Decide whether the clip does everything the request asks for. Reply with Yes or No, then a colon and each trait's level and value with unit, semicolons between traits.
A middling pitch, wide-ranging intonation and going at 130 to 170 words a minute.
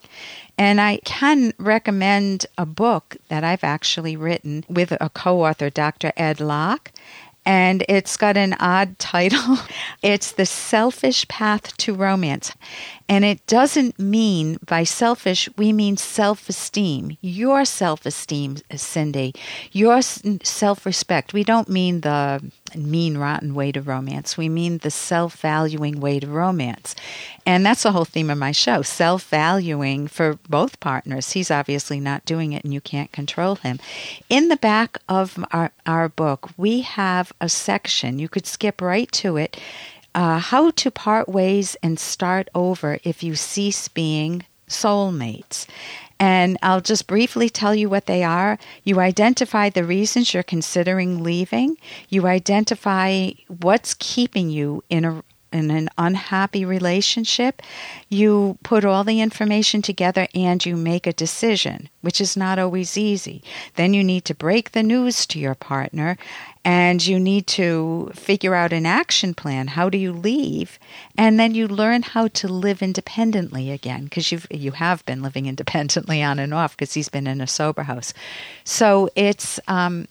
No: medium, 180 Hz; average, 4.5 semitones; average, 155 wpm